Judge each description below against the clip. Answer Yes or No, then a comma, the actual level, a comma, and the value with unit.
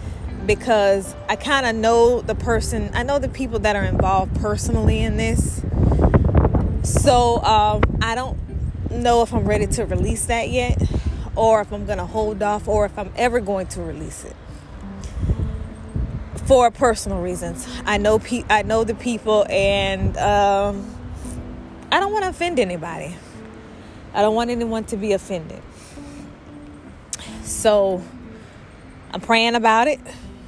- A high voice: Yes, high, 210 Hz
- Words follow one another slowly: No, average, 145 wpm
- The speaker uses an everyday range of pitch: No, wide, 5.7 semitones